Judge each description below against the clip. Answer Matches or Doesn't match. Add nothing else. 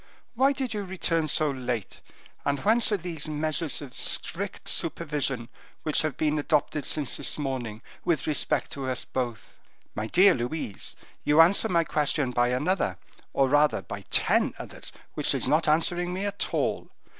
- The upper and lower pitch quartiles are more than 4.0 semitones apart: Matches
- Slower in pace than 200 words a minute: Matches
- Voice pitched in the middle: Matches